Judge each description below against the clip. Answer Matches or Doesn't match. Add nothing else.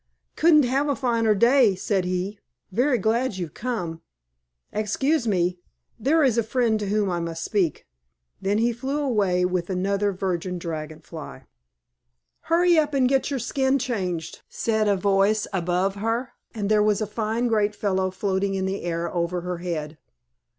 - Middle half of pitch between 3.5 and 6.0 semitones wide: Matches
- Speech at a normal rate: Matches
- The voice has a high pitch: Matches